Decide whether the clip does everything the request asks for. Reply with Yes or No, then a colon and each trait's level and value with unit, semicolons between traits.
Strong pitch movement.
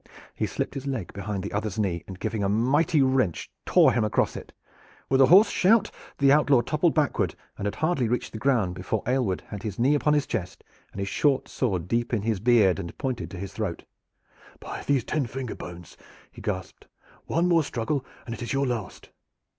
Yes: wide, 5.7 semitones